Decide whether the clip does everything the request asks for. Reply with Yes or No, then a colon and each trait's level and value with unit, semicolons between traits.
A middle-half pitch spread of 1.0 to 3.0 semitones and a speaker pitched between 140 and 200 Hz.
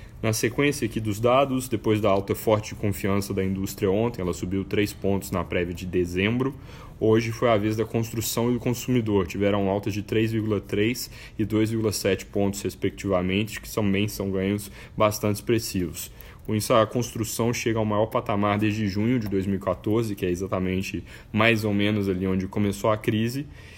No: narrow, 2.5 semitones; low, 105 Hz